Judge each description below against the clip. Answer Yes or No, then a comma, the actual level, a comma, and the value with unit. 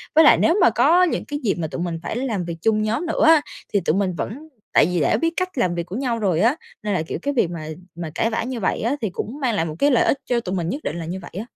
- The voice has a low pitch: No, high, 215 Hz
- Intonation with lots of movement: Yes, wide, 7.5 semitones